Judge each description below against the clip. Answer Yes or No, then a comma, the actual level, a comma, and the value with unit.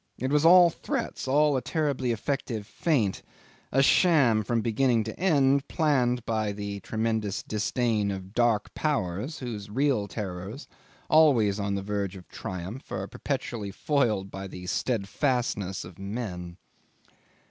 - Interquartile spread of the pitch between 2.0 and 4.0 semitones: No, average, 5.2 semitones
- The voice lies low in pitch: Yes, low, 115 Hz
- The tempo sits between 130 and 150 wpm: Yes, average, 140 wpm